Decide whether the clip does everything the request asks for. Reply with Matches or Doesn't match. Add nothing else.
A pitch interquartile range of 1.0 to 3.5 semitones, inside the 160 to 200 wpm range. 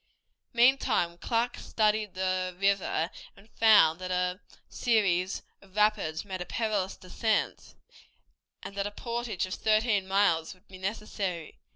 Doesn't match